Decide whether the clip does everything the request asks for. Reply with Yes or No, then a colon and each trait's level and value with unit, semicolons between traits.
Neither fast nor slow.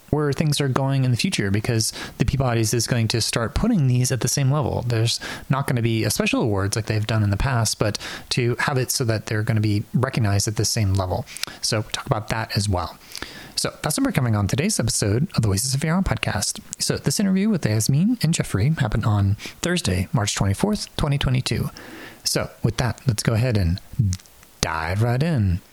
No: fast, 215 wpm